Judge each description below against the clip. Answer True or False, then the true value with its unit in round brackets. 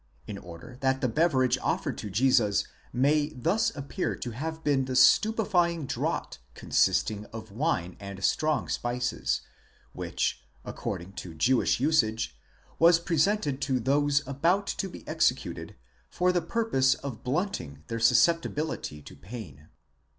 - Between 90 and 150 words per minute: True (135 wpm)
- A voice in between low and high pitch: False (130 Hz)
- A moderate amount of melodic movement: False (6.6 semitones)